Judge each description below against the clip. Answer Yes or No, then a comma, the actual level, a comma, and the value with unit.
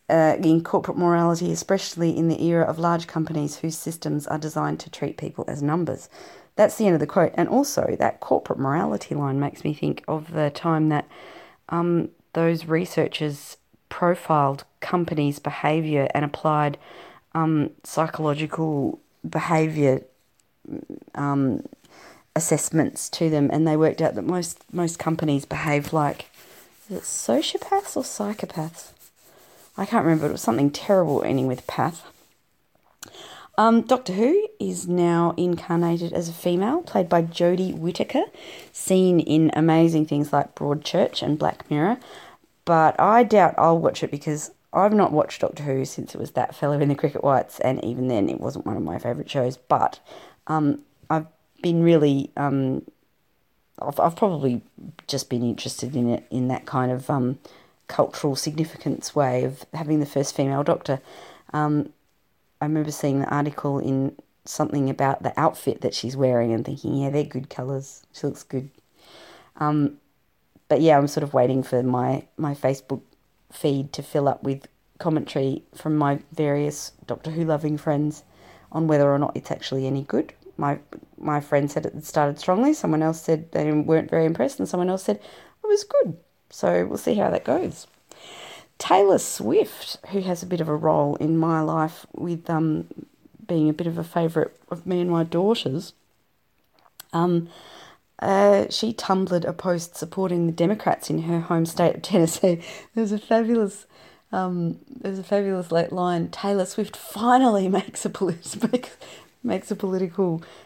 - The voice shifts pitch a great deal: No, average, 3.6 semitones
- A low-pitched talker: No, medium, 160 Hz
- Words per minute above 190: No, average, 165 wpm